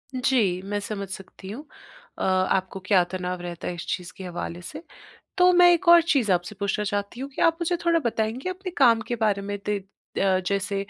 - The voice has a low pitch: No, high, 205 Hz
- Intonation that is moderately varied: No, wide, 6.1 semitones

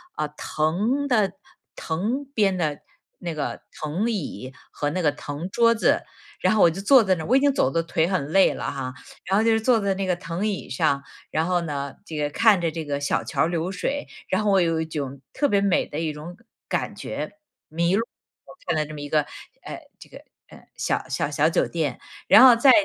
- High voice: No, medium, 170 Hz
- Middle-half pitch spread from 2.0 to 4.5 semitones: No, average, 5.2 semitones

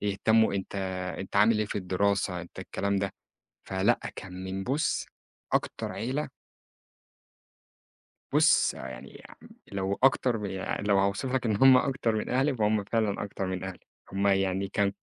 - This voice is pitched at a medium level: No, low, 100 Hz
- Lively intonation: No, average, 2.7 semitones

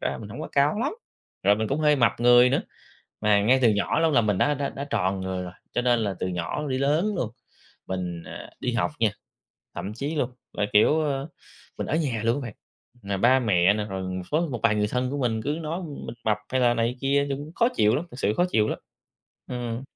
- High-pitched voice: No, low, 120 Hz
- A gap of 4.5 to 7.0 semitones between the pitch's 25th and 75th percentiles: Yes, average, 5.3 semitones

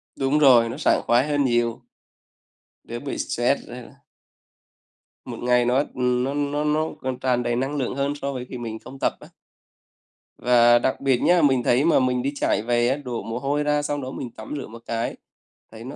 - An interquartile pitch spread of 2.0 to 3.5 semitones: Yes, average, 2.8 semitones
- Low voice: Yes, low, 130 Hz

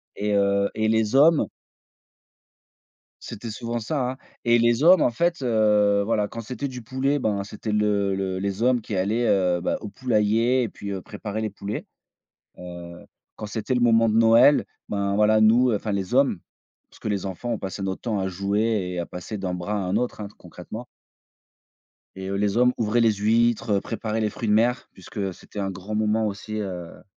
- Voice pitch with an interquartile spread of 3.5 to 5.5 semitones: No, average, 2.9 semitones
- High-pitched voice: No, low, 105 Hz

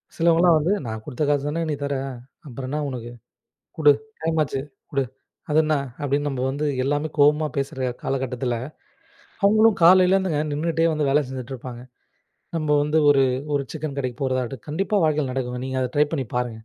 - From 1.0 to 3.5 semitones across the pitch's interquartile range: Yes, average, 3.2 semitones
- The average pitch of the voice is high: No, medium, 145 Hz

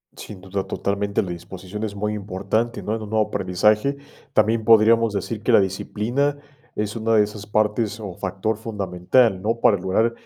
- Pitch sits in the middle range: No, low, 105 Hz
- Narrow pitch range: Yes, narrow, 2.3 semitones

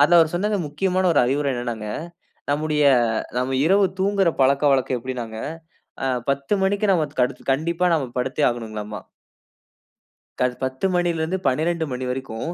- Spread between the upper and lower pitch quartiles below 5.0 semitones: No, wide, 5.4 semitones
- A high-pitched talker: No, medium, 145 Hz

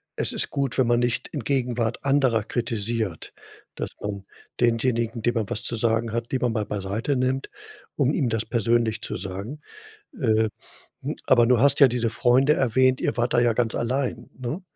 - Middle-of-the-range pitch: No, low, 120 Hz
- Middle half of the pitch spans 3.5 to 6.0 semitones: No, narrow, 2.5 semitones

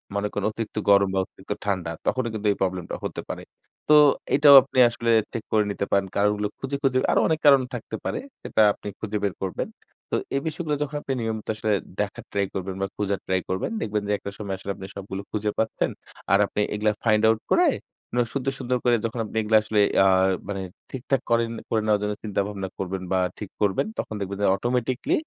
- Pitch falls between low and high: No, low, 105 Hz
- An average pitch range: Yes, average, 3.0 semitones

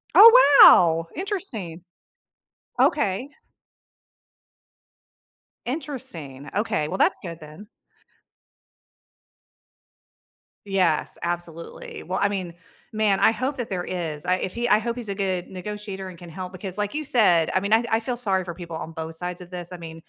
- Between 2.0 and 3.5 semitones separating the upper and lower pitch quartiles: No, average, 4.4 semitones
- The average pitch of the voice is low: No, medium, 185 Hz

